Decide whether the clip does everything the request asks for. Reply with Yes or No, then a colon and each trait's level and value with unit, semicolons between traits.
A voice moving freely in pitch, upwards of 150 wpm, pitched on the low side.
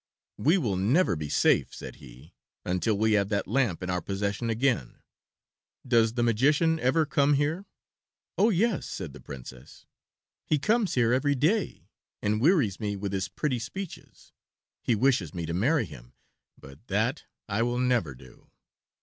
Yes: wide, 7.1 semitones; average, 160 wpm; low, 115 Hz